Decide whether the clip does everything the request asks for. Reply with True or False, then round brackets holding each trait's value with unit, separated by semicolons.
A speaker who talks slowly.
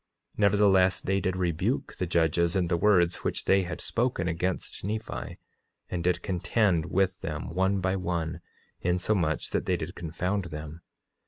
False (155 wpm)